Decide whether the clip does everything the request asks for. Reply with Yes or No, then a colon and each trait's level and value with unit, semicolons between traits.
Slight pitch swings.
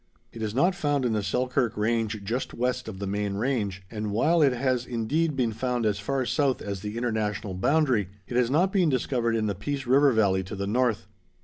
No: average, 4.1 semitones